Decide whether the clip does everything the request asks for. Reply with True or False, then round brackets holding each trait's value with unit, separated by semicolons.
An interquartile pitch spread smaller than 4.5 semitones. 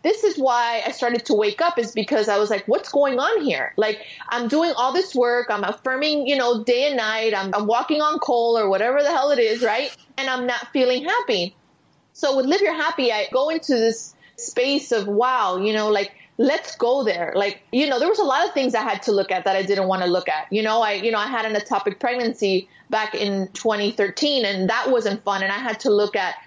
False (5.0 semitones)